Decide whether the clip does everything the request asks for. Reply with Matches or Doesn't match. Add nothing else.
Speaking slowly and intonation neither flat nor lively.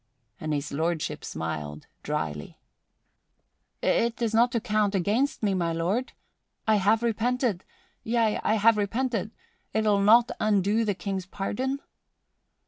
Matches